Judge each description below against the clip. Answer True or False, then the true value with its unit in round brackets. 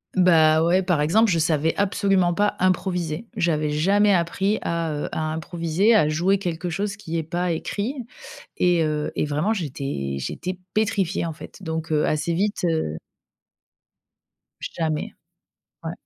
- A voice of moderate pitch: True (170 Hz)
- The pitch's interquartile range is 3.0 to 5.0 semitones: True (3.6 semitones)